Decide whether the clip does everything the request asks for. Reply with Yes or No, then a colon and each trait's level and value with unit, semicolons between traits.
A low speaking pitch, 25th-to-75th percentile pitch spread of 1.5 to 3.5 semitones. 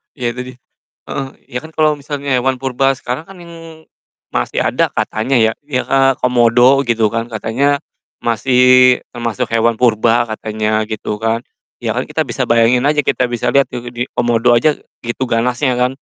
Yes: low, 125 Hz; average, 2.7 semitones